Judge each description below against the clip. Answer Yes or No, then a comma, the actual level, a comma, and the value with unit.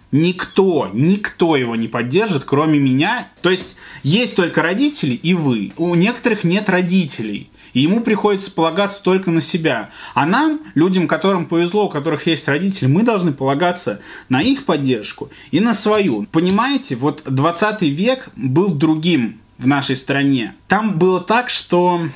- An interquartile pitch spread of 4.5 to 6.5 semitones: Yes, wide, 5.6 semitones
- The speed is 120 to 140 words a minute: No, average, 150 wpm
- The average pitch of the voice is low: No, medium, 175 Hz